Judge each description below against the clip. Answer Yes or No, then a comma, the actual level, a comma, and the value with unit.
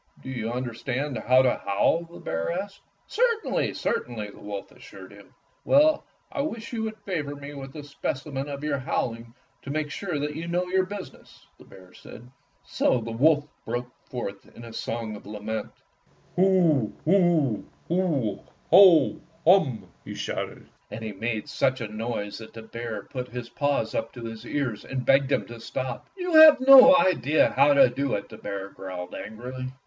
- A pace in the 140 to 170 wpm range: No, average, 180 wpm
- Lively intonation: Yes, wide, 6.8 semitones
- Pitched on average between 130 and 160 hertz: Yes, low, 135 Hz